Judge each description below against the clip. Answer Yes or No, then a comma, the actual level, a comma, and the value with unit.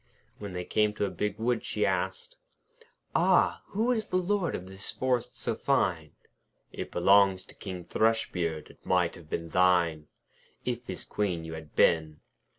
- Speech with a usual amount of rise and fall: No, wide, 5.7 semitones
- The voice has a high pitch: No, very low, 95 Hz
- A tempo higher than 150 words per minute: Yes, average, 165 wpm